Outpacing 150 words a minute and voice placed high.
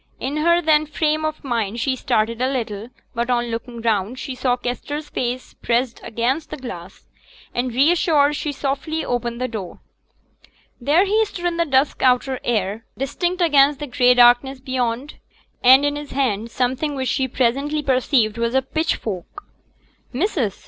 Yes: average, 160 wpm; very high, 260 Hz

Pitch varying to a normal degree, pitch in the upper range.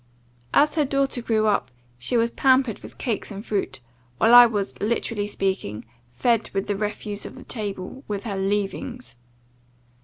Yes: average, 3.4 semitones; high, 215 Hz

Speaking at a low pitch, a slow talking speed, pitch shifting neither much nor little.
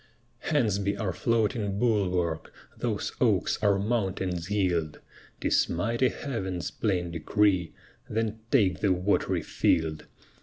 Yes: low, 100 Hz; slow, 115 wpm; average, 3.6 semitones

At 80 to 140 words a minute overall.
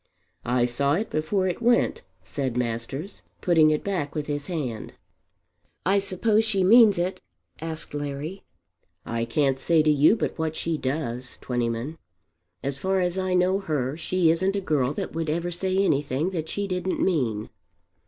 No: average, 165 wpm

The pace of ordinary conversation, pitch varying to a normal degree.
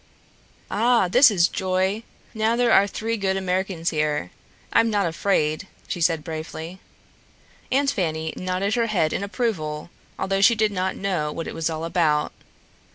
Yes: average, 160 wpm; average, 4.3 semitones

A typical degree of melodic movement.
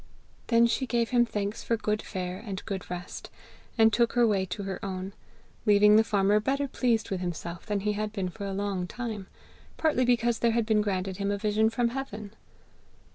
Yes: average, 3.0 semitones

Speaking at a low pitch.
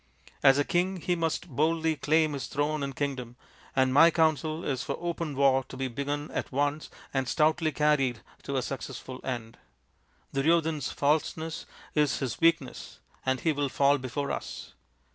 No: medium, 145 Hz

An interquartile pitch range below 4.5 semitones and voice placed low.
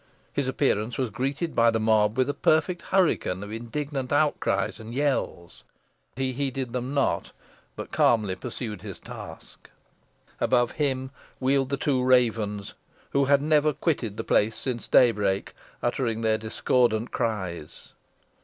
Yes: average, 4.1 semitones; low, 125 Hz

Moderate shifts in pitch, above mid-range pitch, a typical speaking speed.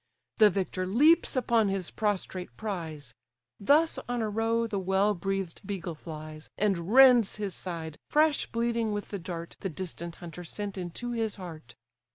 Yes: average, 4.6 semitones; high, 195 Hz; average, 160 wpm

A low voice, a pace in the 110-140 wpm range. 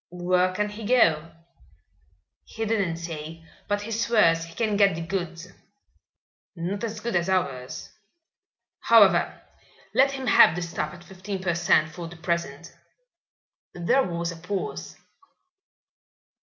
No: medium, 180 Hz; slow, 135 wpm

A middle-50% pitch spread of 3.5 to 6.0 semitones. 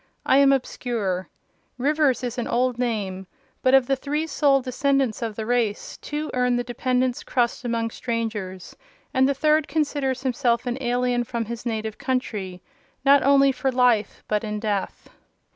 No: average, 2.9 semitones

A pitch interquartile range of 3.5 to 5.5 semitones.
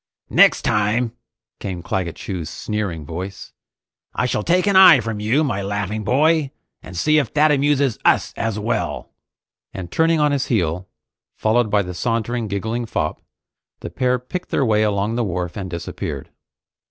Yes: average, 5.0 semitones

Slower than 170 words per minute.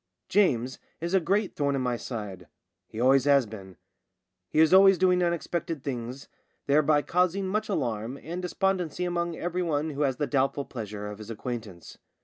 No: average, 175 wpm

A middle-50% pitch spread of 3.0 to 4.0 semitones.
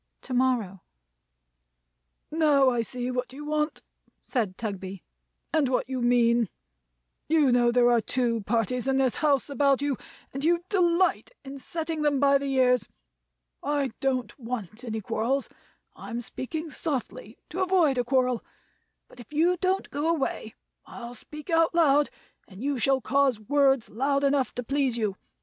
Yes: average, 3.4 semitones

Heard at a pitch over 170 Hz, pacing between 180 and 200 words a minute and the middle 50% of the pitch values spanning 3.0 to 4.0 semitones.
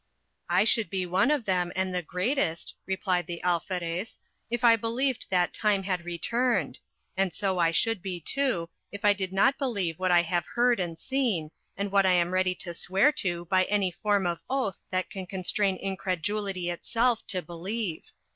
Yes: high, 190 Hz; average, 185 wpm; average, 3.3 semitones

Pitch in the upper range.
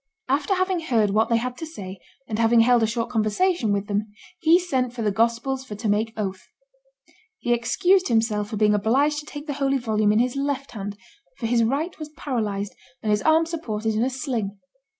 Yes: high, 235 Hz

